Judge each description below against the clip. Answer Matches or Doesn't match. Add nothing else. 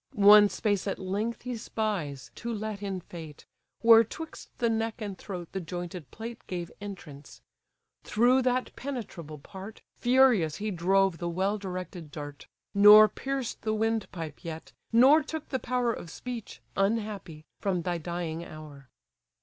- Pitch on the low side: Doesn't match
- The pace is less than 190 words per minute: Matches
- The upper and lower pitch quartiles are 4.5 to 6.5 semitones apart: Matches